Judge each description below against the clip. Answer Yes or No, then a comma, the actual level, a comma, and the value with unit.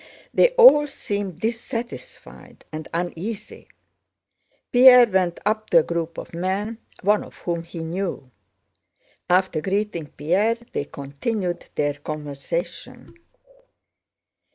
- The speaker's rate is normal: No, slow, 105 wpm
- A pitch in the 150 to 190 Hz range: Yes, medium, 185 Hz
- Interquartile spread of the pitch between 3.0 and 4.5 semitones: No, average, 5.1 semitones